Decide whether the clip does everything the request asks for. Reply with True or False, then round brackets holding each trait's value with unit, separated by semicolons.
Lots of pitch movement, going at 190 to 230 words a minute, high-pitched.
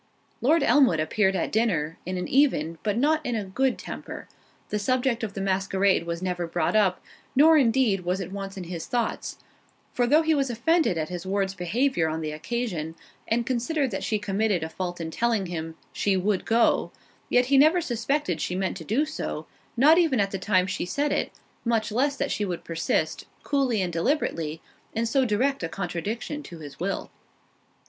True (6.2 semitones; 195 wpm; 205 Hz)